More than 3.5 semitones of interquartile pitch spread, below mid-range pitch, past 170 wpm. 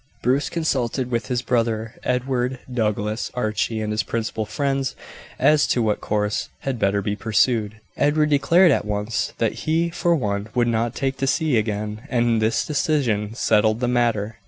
No: average, 3.9 semitones; low, 115 Hz; average, 165 wpm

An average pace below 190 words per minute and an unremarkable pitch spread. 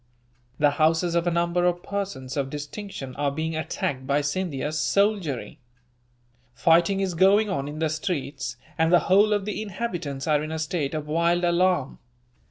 Yes: average, 170 wpm; average, 4.1 semitones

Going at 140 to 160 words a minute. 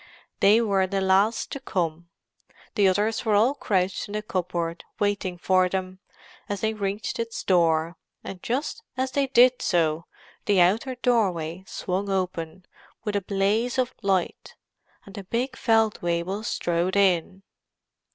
Yes: average, 145 wpm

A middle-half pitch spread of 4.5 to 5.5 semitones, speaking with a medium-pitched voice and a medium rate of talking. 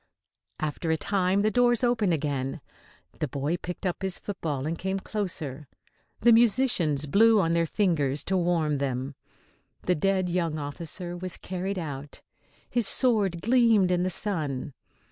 Yes: average, 4.9 semitones; medium, 175 Hz; average, 150 wpm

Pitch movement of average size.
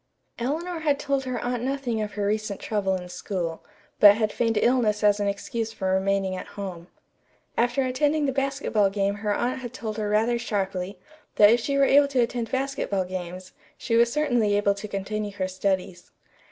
Yes: average, 4.2 semitones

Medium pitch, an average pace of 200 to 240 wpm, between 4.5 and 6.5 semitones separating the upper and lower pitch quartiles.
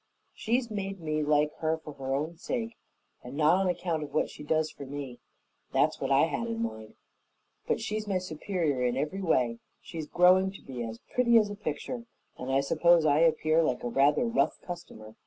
Yes: medium, 160 Hz; fast, 205 wpm; wide, 5.5 semitones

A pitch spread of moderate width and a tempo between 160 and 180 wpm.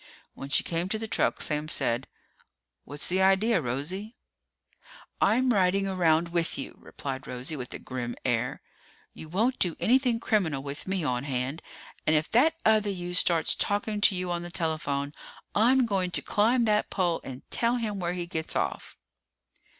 No: wide, 6.1 semitones; average, 175 wpm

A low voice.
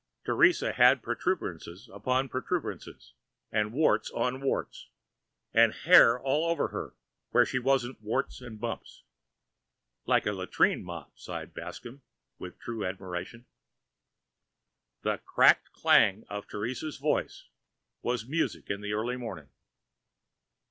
Yes: low, 120 Hz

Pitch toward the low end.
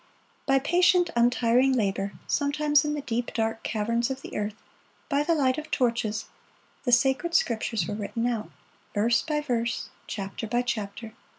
No: high, 240 Hz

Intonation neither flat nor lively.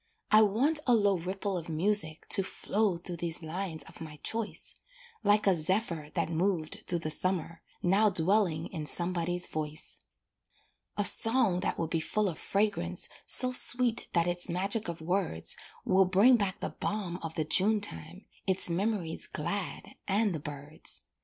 Yes: average, 3.9 semitones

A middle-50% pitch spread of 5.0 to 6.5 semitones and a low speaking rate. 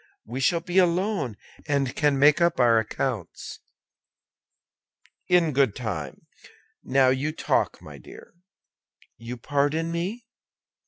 Yes: average, 5.3 semitones; slow, 115 wpm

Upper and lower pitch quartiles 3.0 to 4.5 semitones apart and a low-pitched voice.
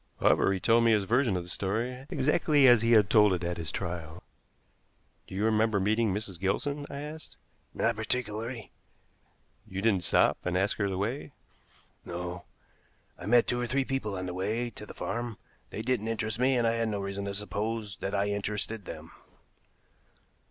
Yes: average, 3.4 semitones; low, 110 Hz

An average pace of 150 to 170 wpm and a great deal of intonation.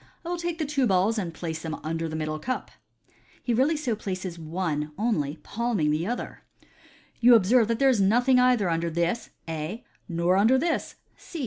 No: average, 195 wpm; wide, 7.0 semitones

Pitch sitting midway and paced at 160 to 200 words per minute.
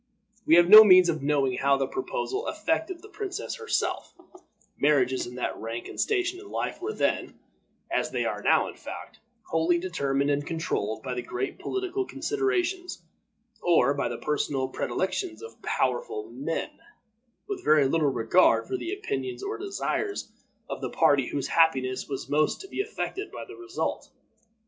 Yes: medium, 180 Hz; average, 165 wpm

